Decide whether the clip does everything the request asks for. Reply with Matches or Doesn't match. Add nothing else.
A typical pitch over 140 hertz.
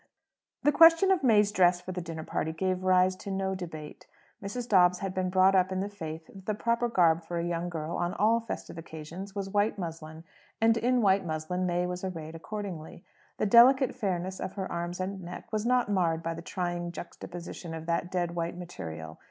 Matches